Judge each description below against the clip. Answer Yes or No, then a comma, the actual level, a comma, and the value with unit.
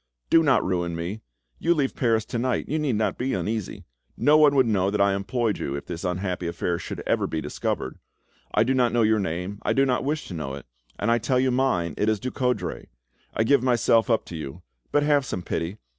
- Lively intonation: Yes, wide, 6.2 semitones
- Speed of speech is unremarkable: No, fast, 230 wpm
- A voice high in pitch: No, low, 110 Hz